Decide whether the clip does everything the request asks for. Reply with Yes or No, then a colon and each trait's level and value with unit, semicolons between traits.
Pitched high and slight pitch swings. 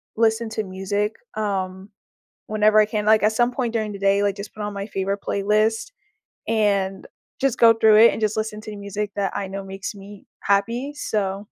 Yes: high, 210 Hz; narrow, 1.7 semitones